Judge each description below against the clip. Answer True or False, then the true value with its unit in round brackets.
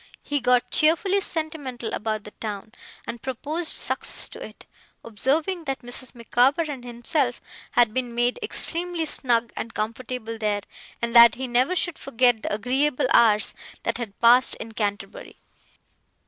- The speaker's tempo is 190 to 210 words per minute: False (145 wpm)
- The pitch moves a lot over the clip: False (4.1 semitones)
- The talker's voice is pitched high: True (245 Hz)